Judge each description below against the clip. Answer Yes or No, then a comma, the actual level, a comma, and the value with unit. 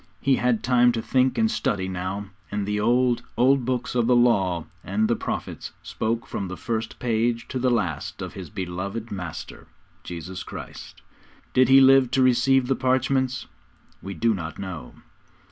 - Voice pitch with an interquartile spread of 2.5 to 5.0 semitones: Yes, average, 4.6 semitones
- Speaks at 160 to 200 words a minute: Yes, average, 170 wpm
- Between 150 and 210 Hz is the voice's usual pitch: No, low, 115 Hz